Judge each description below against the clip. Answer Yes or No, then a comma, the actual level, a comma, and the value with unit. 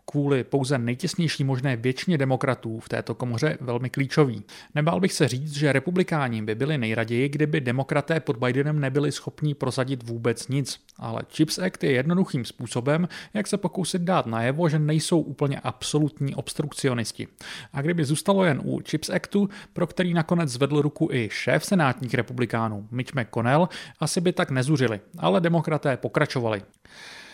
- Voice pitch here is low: No, medium, 145 Hz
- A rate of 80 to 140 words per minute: No, average, 155 wpm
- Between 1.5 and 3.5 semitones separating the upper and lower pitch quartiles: No, average, 4.2 semitones